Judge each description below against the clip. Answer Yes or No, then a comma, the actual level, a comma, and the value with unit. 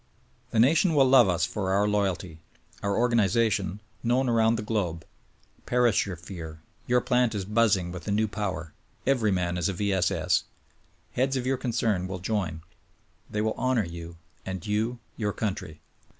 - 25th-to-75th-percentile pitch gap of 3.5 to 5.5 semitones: Yes, average, 4.3 semitones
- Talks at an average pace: Yes, average, 175 wpm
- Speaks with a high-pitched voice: No, low, 105 Hz